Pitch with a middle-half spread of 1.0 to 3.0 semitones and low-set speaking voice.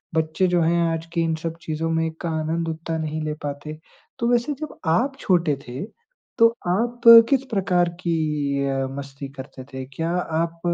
No: narrow, 2.6 semitones; medium, 165 Hz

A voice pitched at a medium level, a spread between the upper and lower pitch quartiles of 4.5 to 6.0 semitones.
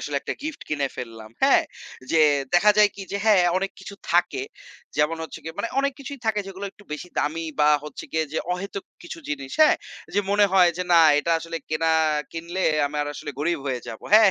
Yes: medium, 175 Hz; average, 5.2 semitones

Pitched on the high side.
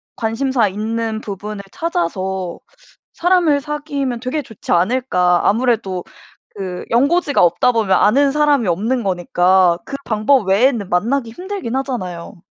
Yes: high, 225 Hz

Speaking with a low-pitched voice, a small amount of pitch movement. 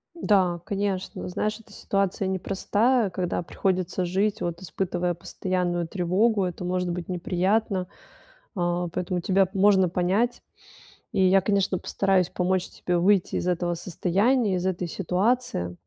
No: medium, 185 Hz; narrow, 2.0 semitones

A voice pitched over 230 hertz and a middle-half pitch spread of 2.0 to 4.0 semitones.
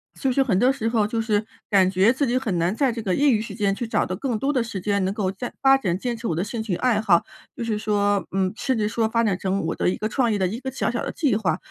No: high, 220 Hz; average, 3.7 semitones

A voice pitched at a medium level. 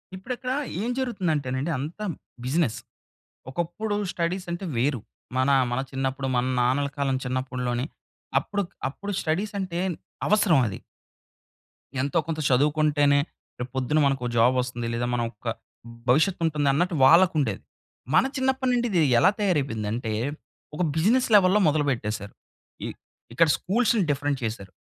Yes: medium, 150 Hz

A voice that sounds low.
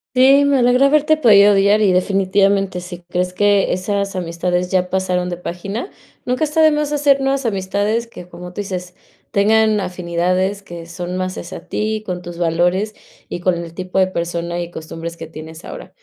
No: medium, 185 Hz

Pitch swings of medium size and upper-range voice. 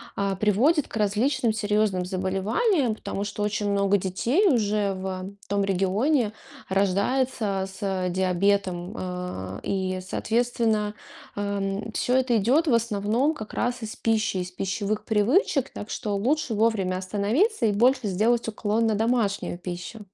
Yes: average, 3.3 semitones; high, 210 Hz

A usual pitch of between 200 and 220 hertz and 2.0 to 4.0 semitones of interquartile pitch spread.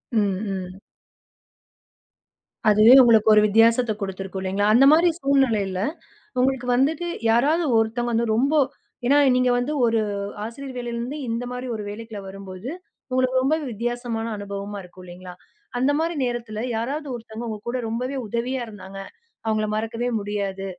No: high, 230 Hz; average, 3.6 semitones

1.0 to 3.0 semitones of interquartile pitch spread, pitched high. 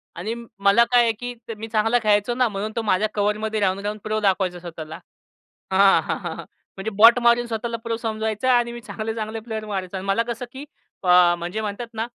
Yes: average, 2.7 semitones; high, 215 Hz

